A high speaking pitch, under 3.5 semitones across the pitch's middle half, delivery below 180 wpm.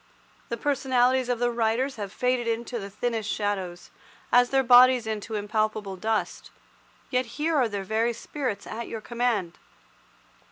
Yes: high, 230 Hz; average, 2.9 semitones; average, 150 wpm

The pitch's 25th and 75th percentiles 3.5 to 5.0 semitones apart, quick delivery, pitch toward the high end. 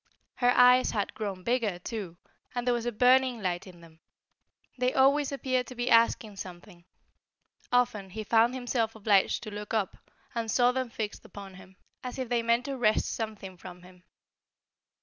No: average, 4.2 semitones; average, 175 wpm; high, 225 Hz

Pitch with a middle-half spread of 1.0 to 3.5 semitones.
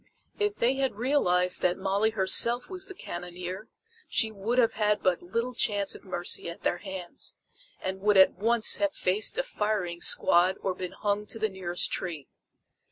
No: average, 4.2 semitones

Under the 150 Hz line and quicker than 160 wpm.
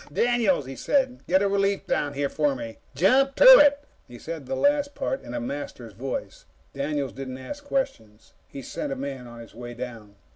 Yes: medium, 140 Hz; average, 195 wpm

